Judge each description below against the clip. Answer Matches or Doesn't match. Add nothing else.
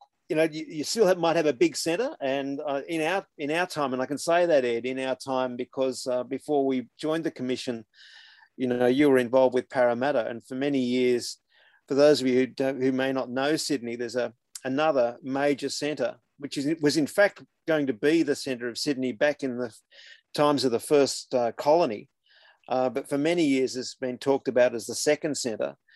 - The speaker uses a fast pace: Matches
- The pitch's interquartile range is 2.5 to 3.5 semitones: Matches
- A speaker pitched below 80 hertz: Doesn't match